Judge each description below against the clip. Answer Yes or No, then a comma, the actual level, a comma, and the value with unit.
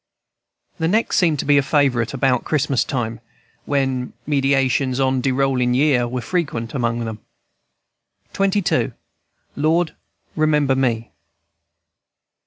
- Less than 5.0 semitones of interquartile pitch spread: Yes, average, 3.2 semitones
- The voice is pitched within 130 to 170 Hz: Yes, low, 135 Hz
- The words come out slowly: Yes, slow, 115 wpm